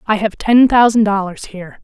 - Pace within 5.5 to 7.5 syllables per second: No, 5.3 syllables/s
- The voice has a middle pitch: No, high, 210 Hz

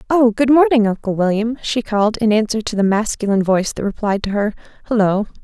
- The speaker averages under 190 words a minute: No, average, 200 wpm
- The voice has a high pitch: Yes, high, 220 Hz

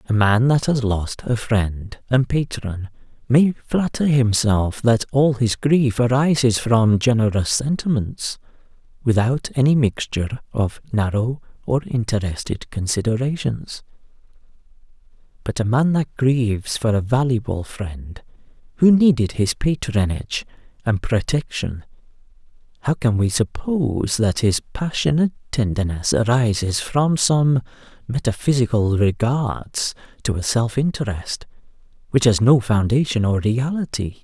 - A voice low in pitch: Yes, low, 120 Hz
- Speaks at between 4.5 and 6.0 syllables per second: No, 4.2 syllables/s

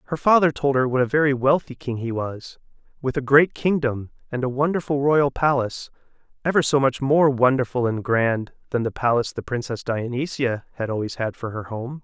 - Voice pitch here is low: Yes, low, 130 Hz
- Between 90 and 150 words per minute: No, average, 195 wpm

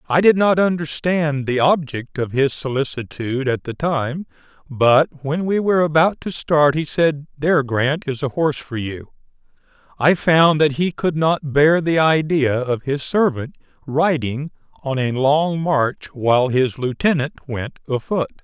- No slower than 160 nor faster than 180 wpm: Yes, average, 165 wpm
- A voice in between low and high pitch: Yes, medium, 145 Hz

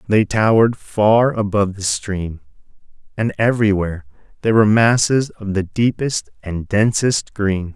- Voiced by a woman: No, male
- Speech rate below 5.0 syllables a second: Yes, 4.7 syllables/s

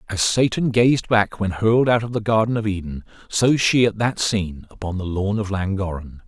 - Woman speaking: No, male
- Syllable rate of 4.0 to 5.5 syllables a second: Yes, 5.2 syllables/s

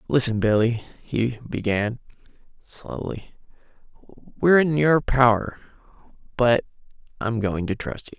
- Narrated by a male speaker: Yes, male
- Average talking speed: No, slow, 110 wpm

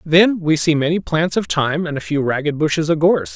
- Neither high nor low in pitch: Yes, medium, 150 Hz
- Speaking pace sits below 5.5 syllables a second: No, 5.9 syllables/s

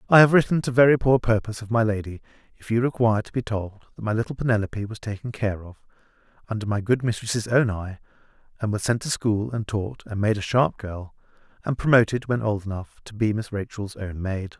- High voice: No, low, 110 Hz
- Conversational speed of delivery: No, fast, 220 wpm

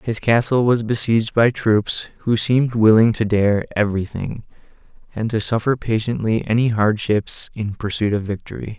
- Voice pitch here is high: No, low, 110 Hz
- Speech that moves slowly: No, average, 155 wpm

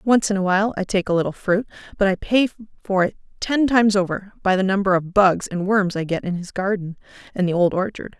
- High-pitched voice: Yes, high, 195 Hz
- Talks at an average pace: No, fast, 240 wpm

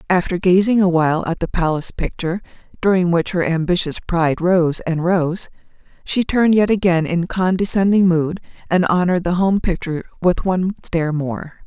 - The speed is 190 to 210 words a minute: No, average, 165 wpm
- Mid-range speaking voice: Yes, medium, 175 Hz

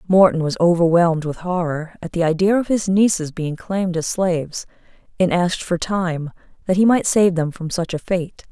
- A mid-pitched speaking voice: Yes, medium, 175 Hz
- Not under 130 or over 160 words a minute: No, average, 195 wpm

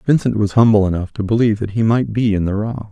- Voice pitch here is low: Yes, low, 110 Hz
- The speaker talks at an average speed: No, fast, 265 wpm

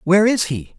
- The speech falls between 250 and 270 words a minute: No, fast, 230 wpm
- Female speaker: No, male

